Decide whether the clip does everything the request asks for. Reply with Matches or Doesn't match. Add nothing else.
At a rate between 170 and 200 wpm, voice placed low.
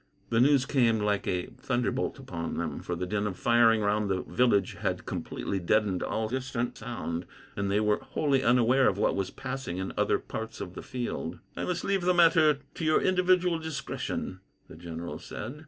Matches